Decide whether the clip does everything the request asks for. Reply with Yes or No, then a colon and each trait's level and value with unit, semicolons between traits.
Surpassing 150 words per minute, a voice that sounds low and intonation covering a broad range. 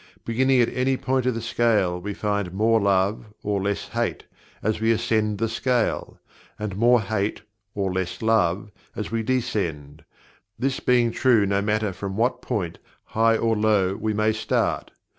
No: average, 165 wpm; low, 110 Hz; narrow, 2.5 semitones